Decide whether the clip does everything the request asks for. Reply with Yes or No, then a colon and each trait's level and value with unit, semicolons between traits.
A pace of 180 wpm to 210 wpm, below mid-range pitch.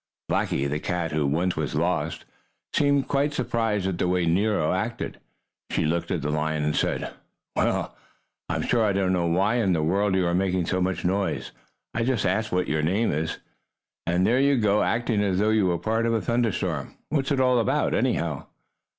Yes: average, 200 wpm; very low, 95 Hz